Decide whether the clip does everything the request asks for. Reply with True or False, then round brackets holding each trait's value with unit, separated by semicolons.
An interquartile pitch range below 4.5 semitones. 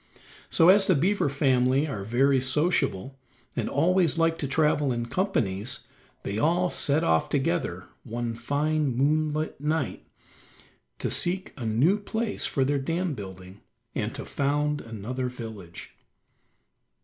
False (5.3 semitones)